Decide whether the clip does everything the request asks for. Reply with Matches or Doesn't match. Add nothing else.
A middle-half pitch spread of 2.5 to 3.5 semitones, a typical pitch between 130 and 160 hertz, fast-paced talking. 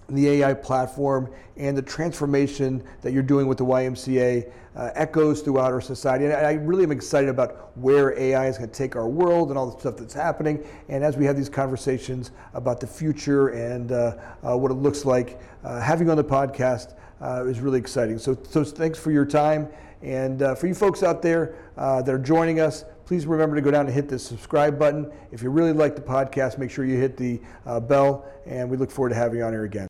Matches